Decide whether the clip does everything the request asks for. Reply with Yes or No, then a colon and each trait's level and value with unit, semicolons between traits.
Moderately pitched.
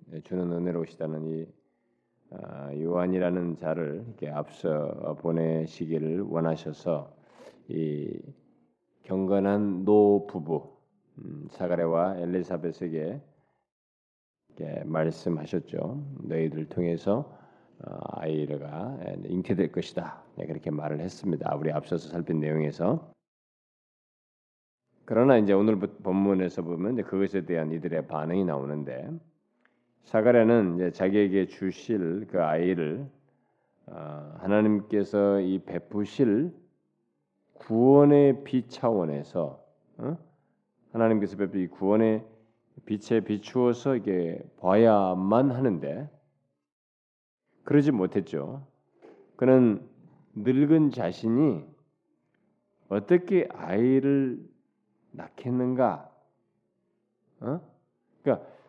No: very low, 95 Hz